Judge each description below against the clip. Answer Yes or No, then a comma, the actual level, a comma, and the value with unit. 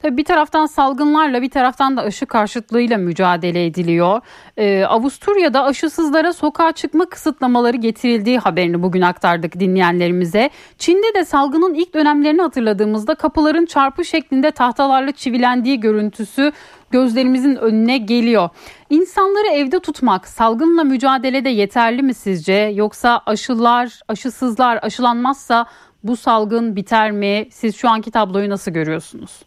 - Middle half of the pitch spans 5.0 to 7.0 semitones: Yes, wide, 5.5 semitones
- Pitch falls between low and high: No, high, 245 Hz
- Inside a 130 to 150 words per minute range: No, average, 120 wpm